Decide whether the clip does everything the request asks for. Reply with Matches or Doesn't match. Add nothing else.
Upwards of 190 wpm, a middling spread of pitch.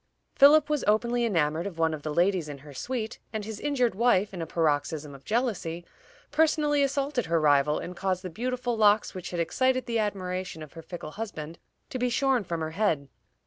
Doesn't match